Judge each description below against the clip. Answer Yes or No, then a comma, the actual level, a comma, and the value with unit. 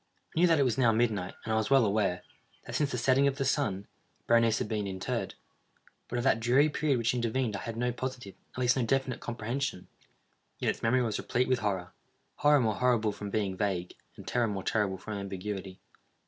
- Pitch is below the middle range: Yes, low, 115 Hz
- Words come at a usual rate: No, fast, 210 wpm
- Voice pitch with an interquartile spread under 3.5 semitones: No, average, 3.9 semitones